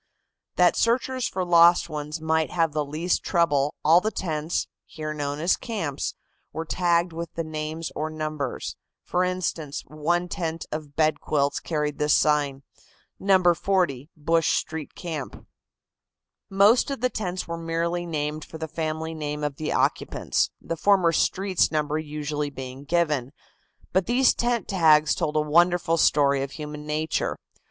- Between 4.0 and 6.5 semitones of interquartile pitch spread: No, average, 2.7 semitones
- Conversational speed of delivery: Yes, average, 155 wpm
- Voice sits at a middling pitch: Yes, medium, 160 Hz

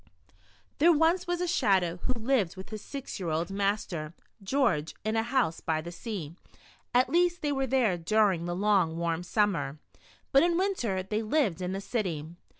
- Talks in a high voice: Yes, high, 205 Hz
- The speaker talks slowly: No, average, 185 wpm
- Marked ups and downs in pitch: Yes, wide, 7.4 semitones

